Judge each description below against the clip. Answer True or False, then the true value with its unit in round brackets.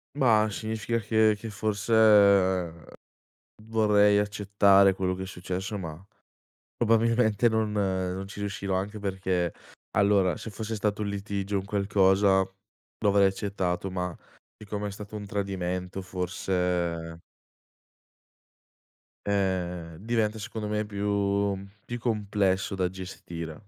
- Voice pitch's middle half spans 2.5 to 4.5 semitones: False (2.1 semitones)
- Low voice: True (100 Hz)